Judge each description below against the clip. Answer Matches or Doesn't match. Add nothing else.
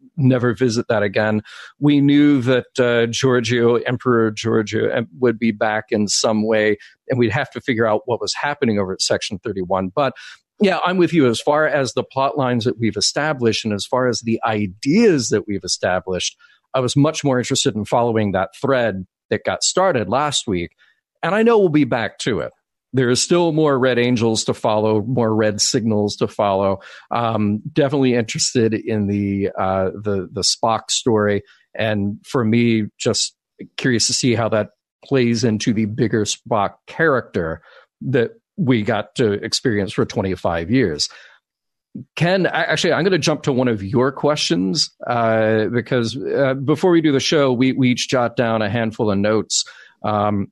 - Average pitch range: Matches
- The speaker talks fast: Doesn't match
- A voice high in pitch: Doesn't match